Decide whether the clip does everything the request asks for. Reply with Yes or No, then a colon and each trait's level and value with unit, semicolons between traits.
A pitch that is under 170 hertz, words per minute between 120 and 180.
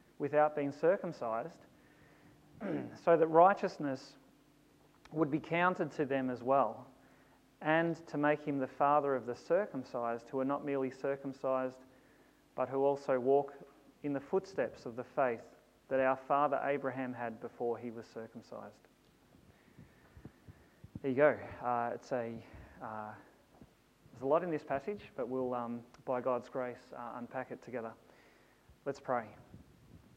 Yes: low, 135 Hz; average, 140 wpm